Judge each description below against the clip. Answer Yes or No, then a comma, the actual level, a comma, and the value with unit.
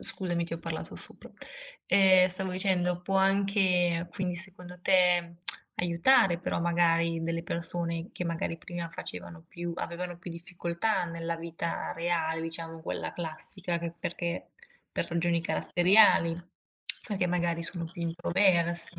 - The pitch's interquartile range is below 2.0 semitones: Yes, narrow, 1.2 semitones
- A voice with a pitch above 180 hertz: No, medium, 175 Hz